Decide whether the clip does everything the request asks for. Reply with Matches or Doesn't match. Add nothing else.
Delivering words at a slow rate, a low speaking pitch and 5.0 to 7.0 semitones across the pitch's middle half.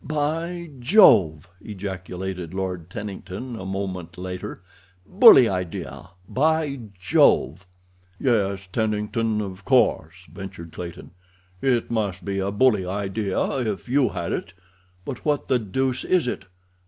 Matches